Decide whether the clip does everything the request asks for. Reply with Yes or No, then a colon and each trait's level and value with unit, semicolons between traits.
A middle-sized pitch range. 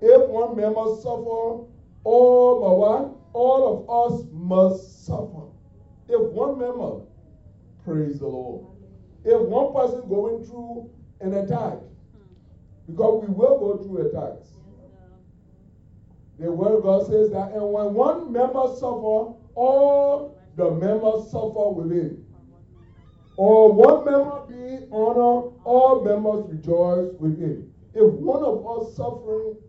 No: wide, 6.2 semitones